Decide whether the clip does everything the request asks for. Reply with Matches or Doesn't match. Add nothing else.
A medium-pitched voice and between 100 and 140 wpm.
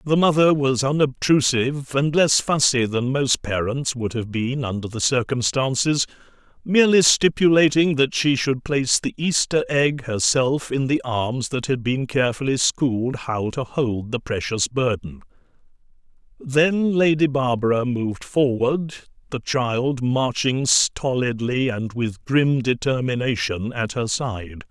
Doesn't match